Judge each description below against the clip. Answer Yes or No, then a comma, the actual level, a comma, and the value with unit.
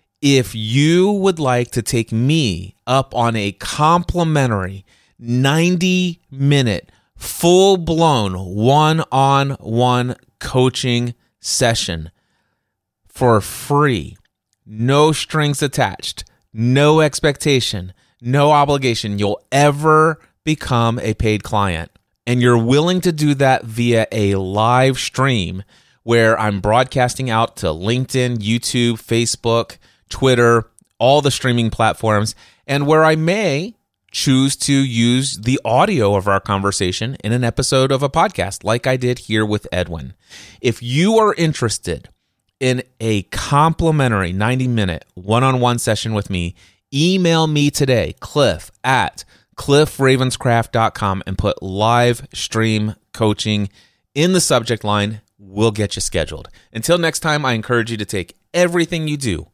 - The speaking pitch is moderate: No, low, 120 Hz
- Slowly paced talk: Yes, slow, 125 wpm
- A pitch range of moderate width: Yes, average, 4.9 semitones